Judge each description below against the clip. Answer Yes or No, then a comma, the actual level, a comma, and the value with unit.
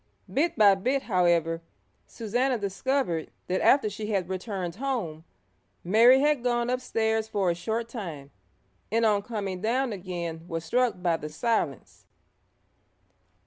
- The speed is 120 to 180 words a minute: Yes, slow, 135 wpm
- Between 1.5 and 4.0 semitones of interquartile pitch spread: No, wide, 5.4 semitones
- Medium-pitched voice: No, high, 210 Hz